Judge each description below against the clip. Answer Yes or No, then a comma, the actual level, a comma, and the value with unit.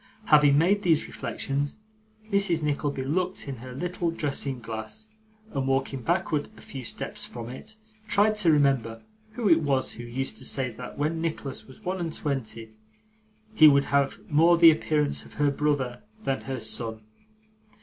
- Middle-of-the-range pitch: Yes, medium, 145 Hz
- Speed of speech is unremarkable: Yes, average, 165 wpm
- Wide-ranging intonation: No, average, 4.1 semitones